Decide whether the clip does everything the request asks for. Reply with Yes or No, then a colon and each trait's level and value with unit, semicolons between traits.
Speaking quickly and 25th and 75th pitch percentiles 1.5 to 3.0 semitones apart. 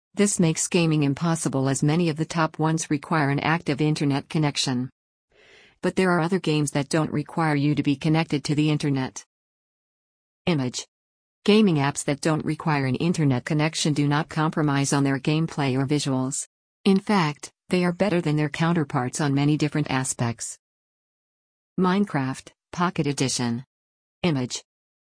No: average, 150 wpm; average, 2.7 semitones